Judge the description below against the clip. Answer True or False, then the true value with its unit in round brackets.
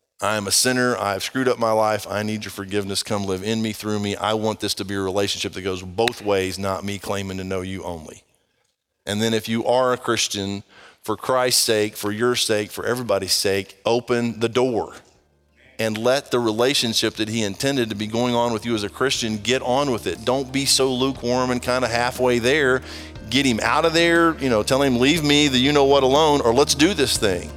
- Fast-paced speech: True (235 wpm)